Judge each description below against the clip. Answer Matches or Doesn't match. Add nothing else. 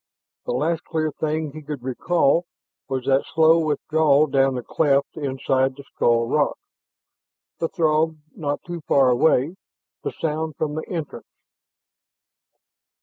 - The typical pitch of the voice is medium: Matches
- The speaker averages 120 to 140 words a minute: Matches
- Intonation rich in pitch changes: Doesn't match